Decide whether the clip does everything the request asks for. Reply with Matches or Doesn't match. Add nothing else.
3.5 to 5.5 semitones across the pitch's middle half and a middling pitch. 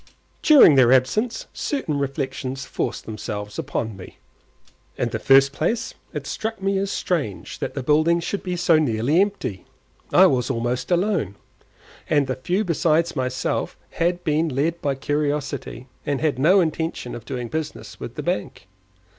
Matches